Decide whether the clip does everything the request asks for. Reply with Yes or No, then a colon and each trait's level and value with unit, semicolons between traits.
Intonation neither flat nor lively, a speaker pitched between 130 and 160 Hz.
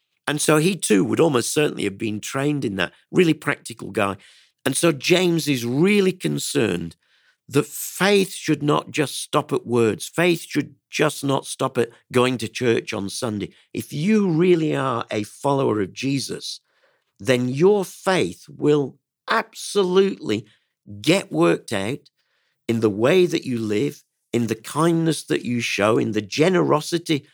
No: wide, 6.4 semitones; medium, 140 Hz